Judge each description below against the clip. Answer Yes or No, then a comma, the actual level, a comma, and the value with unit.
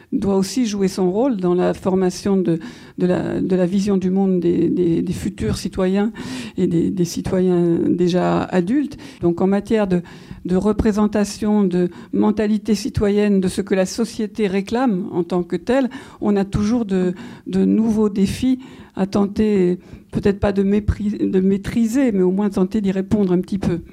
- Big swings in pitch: No, average, 2.8 semitones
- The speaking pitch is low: No, high, 195 Hz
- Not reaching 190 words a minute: Yes, average, 175 wpm